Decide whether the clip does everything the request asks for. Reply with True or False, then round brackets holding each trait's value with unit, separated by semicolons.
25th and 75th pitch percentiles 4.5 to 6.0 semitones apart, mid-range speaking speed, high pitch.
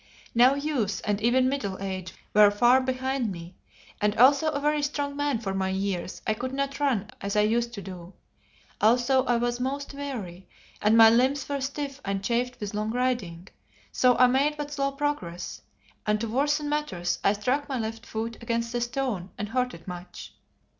True (5.0 semitones; 190 wpm; 240 Hz)